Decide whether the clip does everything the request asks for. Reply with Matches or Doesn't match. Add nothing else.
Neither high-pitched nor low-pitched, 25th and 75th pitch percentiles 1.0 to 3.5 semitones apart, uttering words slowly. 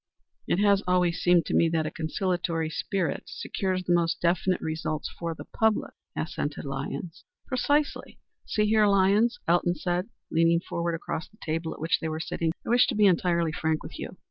Doesn't match